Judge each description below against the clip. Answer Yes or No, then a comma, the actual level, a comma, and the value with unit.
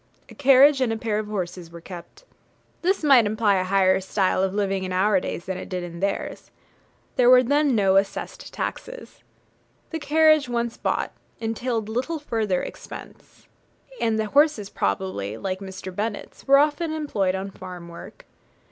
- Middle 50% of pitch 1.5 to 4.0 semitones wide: No, wide, 5.6 semitones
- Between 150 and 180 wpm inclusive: Yes, average, 165 wpm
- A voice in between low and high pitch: No, high, 210 Hz